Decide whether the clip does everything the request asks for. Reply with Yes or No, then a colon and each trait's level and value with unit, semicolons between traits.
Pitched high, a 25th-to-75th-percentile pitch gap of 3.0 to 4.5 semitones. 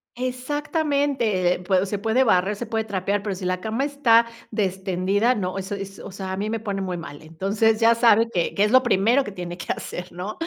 Yes: high, 205 Hz; average, 3.8 semitones